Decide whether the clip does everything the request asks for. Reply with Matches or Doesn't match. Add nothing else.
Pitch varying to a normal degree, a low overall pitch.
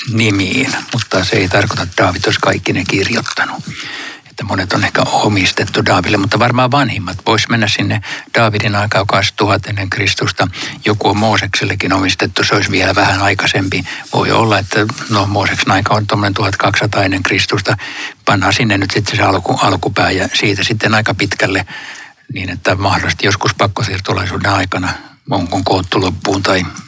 Doesn't match